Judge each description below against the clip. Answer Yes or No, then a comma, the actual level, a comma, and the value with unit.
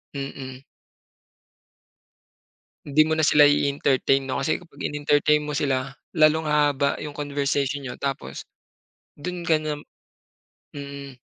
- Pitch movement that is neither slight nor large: No, narrow, 1.6 semitones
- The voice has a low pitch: No, medium, 145 Hz